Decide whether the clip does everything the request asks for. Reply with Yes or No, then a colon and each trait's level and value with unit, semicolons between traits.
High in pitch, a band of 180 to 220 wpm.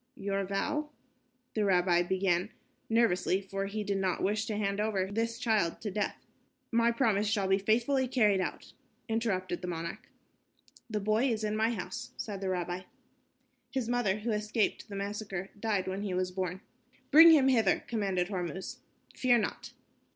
No: high, 205 Hz; average, 165 wpm